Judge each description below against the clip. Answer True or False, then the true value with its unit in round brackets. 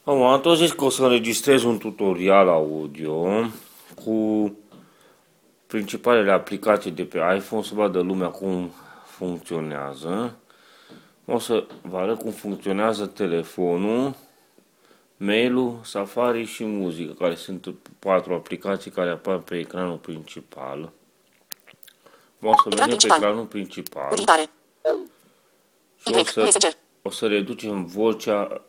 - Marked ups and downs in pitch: False (4.4 semitones)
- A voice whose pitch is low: True (100 Hz)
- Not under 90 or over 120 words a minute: True (115 wpm)